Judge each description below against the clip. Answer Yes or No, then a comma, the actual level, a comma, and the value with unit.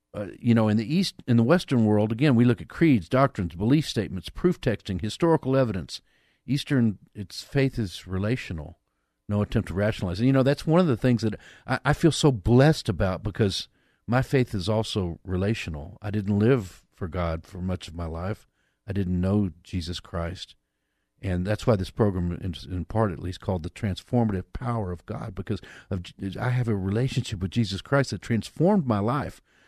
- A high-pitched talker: No, low, 105 Hz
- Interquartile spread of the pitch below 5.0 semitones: No, average, 5.3 semitones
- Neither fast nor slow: Yes, average, 195 wpm